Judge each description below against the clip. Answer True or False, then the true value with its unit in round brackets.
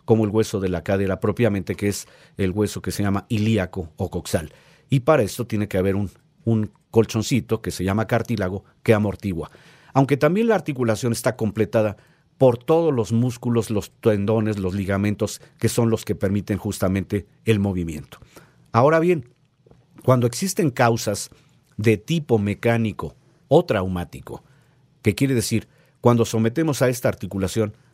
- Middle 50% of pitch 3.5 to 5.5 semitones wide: True (4.5 semitones)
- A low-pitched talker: True (110 Hz)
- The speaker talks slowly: False (155 wpm)